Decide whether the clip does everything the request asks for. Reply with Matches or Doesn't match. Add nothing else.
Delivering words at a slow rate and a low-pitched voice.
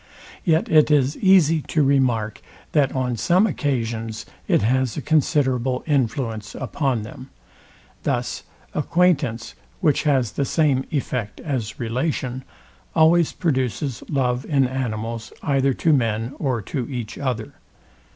Matches